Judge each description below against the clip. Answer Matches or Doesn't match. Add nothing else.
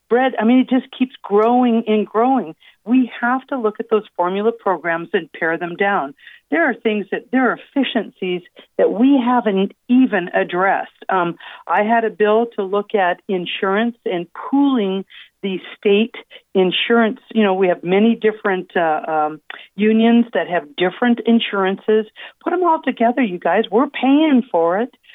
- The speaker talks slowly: Doesn't match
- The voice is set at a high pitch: Matches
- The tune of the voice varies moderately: Matches